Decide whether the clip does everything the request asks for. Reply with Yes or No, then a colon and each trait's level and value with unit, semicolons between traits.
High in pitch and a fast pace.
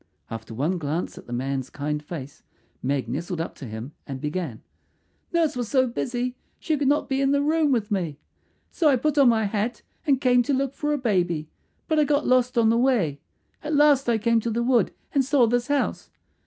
Yes: high, 235 Hz; fast, 215 wpm